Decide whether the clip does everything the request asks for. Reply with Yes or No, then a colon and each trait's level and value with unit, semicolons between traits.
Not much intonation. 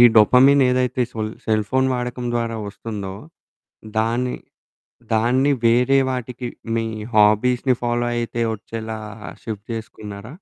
Yes: narrow, 2.3 semitones